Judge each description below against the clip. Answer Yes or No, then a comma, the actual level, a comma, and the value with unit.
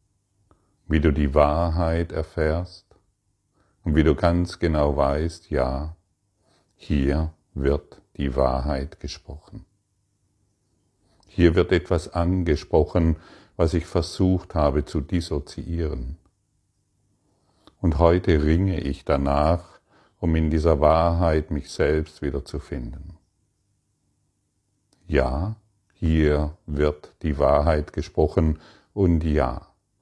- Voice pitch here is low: Yes, very low, 85 Hz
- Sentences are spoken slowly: Yes, slow, 95 wpm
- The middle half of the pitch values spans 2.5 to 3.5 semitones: No, average, 4.3 semitones